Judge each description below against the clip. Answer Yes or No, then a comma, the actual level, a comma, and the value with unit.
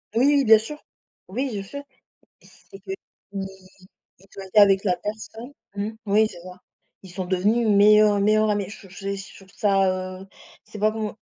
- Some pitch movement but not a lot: No, narrow, 2.0 semitones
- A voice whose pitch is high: Yes, high, 205 Hz